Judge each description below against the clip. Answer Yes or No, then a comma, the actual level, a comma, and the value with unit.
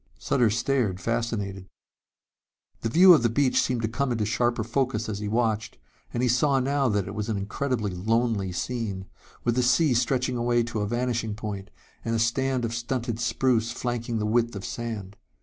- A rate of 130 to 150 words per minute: No, average, 185 wpm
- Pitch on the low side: Yes, low, 115 Hz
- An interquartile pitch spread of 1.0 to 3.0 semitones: Yes, narrow, 2.6 semitones